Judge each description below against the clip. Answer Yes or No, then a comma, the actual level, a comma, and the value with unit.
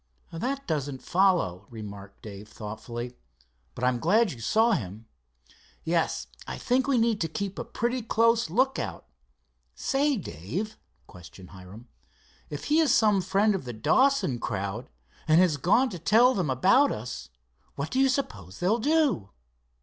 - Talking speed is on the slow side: No, average, 150 wpm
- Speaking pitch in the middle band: Yes, medium, 175 Hz